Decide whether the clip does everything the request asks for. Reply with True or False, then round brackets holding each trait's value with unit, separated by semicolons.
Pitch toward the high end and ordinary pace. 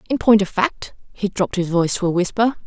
False (200 Hz; 250 wpm)